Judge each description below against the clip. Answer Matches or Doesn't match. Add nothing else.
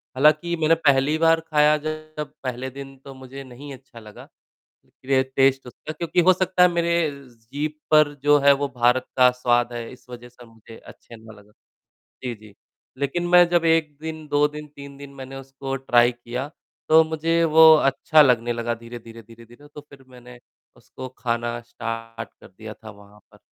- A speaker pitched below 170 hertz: Matches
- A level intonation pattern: Doesn't match